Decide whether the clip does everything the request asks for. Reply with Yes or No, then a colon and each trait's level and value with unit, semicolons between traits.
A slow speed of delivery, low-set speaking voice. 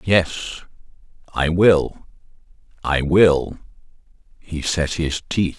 Yes: slow, 75 wpm; very low, 80 Hz